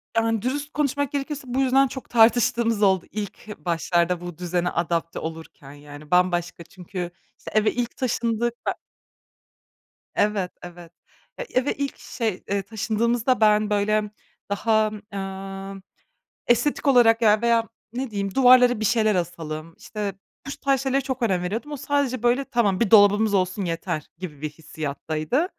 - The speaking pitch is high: Yes, high, 210 Hz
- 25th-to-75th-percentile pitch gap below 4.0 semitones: No, average, 5.2 semitones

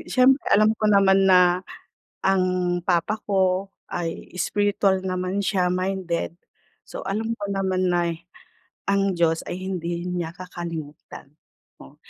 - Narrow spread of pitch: Yes, narrow, 2.0 semitones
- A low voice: No, medium, 185 Hz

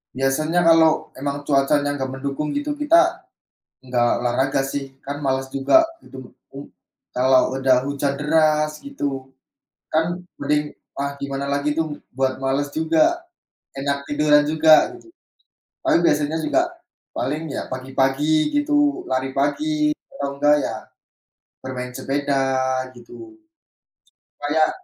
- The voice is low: No, medium, 145 Hz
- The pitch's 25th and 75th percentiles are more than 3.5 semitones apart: No, average, 2.9 semitones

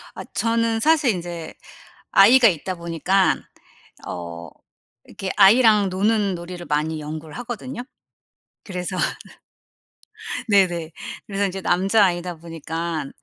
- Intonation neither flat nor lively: Yes, average, 4.0 semitones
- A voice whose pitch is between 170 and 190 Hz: Yes, medium, 185 Hz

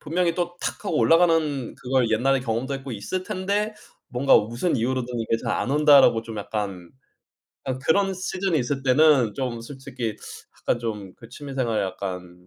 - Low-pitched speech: Yes, low, 130 Hz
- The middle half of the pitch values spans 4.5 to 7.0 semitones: Yes, wide, 5.4 semitones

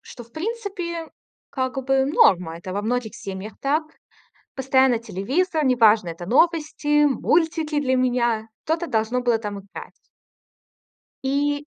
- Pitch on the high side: Yes, very high, 260 Hz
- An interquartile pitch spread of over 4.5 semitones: Yes, wide, 5.5 semitones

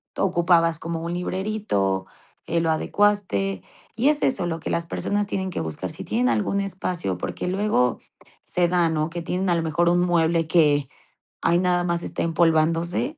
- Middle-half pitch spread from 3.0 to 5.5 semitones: No, narrow, 2.5 semitones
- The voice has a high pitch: No, medium, 170 Hz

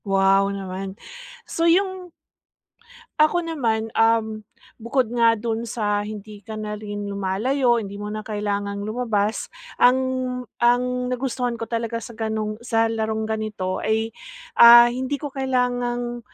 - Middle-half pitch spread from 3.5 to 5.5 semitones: No, average, 2.7 semitones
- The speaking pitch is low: No, high, 225 Hz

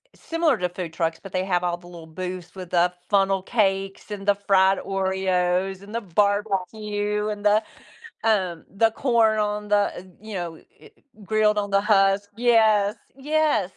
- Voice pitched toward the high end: Yes, high, 200 Hz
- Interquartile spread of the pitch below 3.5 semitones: Yes, narrow, 2.4 semitones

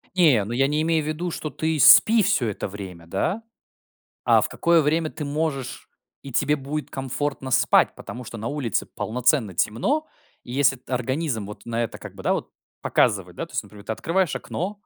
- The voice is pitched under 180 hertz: Yes, low, 135 Hz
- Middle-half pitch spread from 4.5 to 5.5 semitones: Yes, average, 5.2 semitones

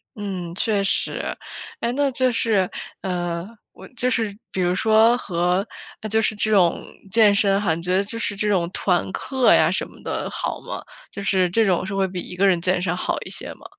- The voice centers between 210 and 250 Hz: No, high, 195 Hz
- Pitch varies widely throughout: No, average, 3.3 semitones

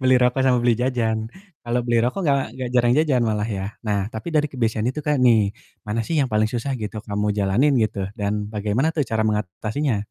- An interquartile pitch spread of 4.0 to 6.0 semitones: No, average, 3.6 semitones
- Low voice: Yes, low, 115 Hz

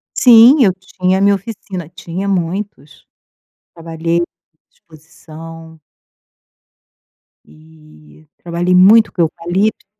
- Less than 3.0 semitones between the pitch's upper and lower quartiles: No, average, 3.3 semitones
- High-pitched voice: No, medium, 175 Hz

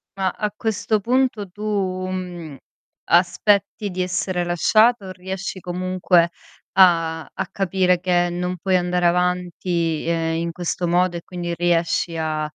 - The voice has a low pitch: No, medium, 180 Hz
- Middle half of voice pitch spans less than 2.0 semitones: Yes, narrow, 1.6 semitones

